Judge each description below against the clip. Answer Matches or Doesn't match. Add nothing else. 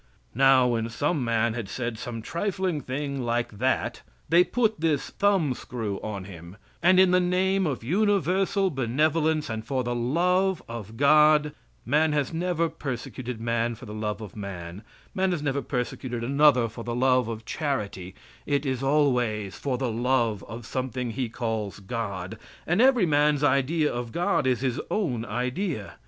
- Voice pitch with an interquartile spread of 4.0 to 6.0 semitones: Matches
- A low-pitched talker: Matches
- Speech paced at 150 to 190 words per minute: Matches